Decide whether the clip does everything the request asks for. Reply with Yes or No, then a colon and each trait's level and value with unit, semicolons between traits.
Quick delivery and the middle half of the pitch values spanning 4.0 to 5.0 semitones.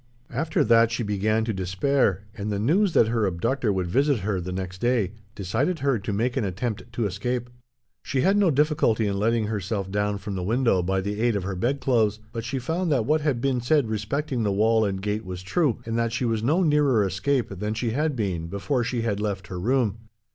Yes: fast, 220 wpm; average, 4.5 semitones